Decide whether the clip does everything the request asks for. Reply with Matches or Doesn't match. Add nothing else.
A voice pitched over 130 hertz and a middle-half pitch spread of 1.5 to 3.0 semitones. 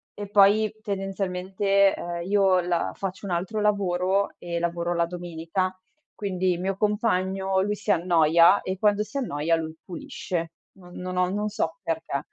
Matches